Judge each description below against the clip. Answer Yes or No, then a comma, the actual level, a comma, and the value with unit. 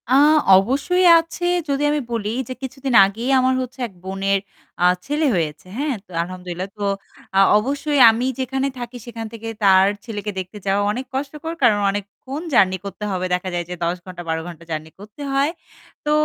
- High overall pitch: Yes, high, 220 Hz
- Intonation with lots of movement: Yes, wide, 6.2 semitones